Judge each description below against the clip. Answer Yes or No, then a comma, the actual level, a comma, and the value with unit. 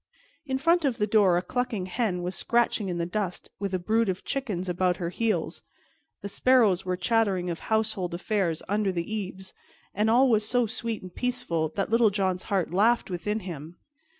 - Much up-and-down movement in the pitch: No, average, 3.9 semitones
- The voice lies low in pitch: No, high, 200 Hz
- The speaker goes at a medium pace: Yes, average, 190 wpm